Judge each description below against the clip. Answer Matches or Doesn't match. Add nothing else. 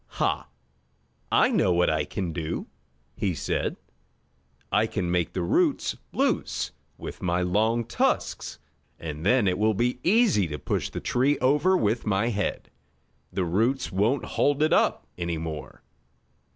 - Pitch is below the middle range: Matches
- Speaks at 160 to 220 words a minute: Doesn't match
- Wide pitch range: Matches